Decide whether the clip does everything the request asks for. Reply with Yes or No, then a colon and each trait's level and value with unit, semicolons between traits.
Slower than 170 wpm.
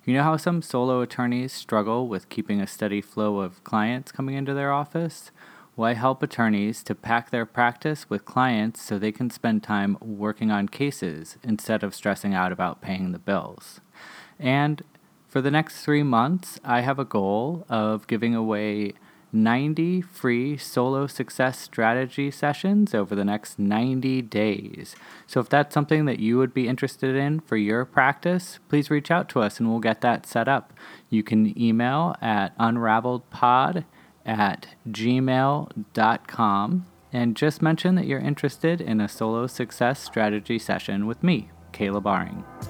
Yes: average, 160 wpm